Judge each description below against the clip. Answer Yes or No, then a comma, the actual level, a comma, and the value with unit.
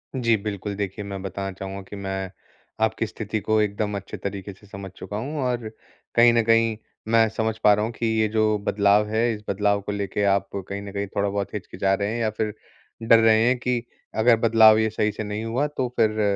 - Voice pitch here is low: Yes, low, 105 Hz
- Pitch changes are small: Yes, narrow, 2.0 semitones